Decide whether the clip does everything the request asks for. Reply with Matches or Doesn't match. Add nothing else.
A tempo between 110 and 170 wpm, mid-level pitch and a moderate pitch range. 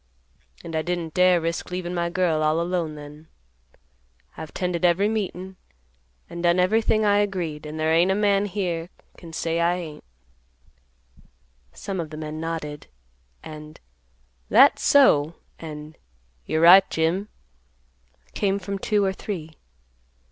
Matches